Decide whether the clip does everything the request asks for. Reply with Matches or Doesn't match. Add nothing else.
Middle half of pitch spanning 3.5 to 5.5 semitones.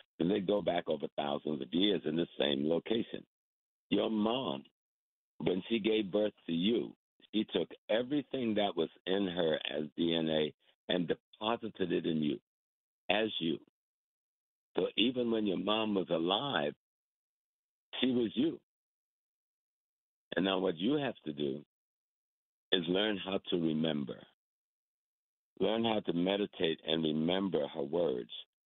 Matches